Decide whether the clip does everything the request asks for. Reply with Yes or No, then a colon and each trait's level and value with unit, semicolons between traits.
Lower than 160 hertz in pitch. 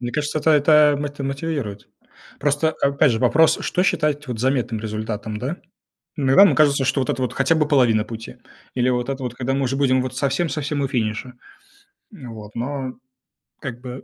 Yes: low, 135 Hz